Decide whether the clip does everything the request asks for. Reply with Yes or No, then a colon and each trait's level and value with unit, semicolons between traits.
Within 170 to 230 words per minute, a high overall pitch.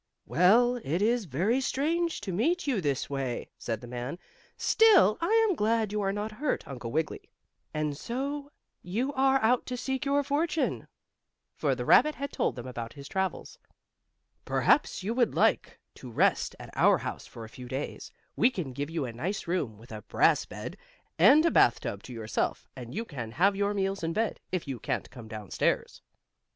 Yes: average, 190 wpm; high, 195 Hz